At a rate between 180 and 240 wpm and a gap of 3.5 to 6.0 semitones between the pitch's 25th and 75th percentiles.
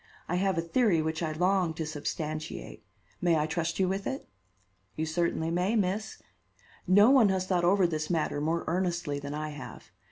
No: average, 185 wpm; average, 3.1 semitones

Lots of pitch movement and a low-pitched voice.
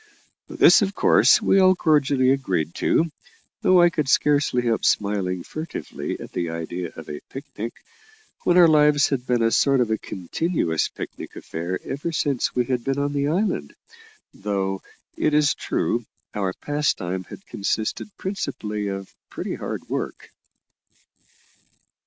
Yes: wide, 7.4 semitones; low, 130 Hz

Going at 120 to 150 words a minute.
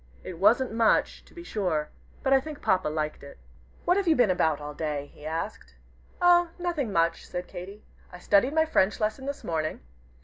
No: average, 195 wpm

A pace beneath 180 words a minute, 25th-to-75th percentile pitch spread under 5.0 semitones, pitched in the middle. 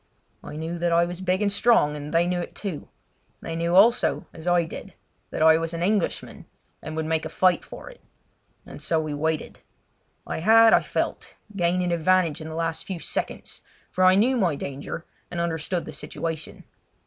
No: average, 195 wpm; narrow, 2.6 semitones; medium, 170 Hz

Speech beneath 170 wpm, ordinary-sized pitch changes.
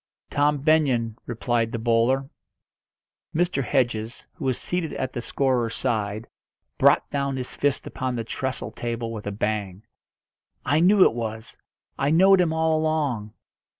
Yes: average, 150 wpm; average, 4.5 semitones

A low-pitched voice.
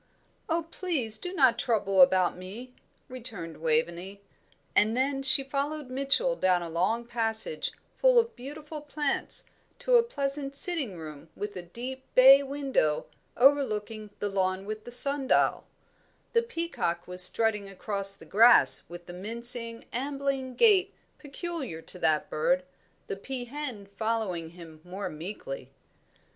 No: high, 235 Hz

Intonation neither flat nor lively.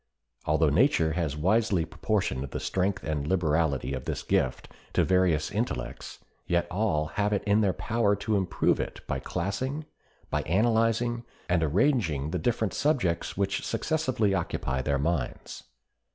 No: wide, 5.9 semitones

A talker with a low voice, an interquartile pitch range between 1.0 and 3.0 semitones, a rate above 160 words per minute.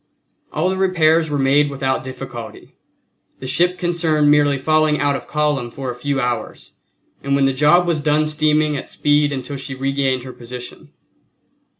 No: medium, 145 Hz; narrow, 2.5 semitones; average, 170 wpm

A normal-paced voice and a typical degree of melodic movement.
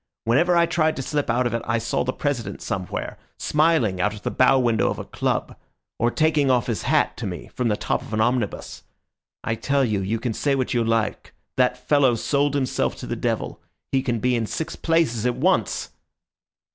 No: fast, 210 wpm; average, 3.9 semitones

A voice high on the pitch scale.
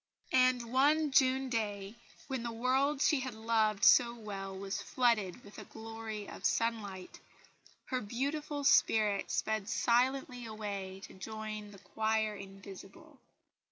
Yes: high, 225 Hz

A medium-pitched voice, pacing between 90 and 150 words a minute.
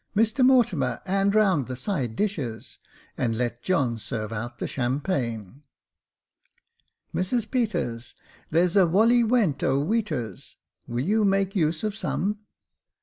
Yes: medium, 170 Hz; slow, 135 wpm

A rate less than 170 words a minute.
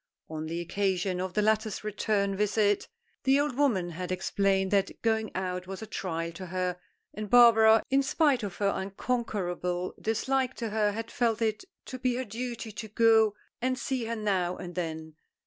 No: average, 180 wpm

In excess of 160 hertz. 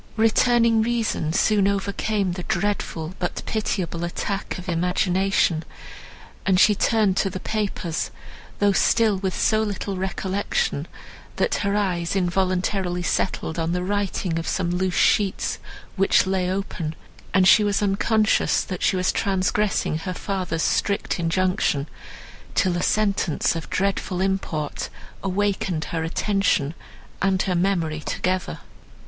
Yes: high, 190 Hz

